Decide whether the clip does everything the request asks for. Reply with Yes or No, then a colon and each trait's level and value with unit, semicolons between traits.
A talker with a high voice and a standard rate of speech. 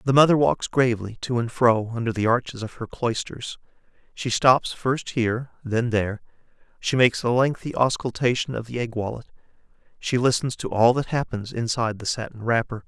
No: low, 120 Hz; average, 175 wpm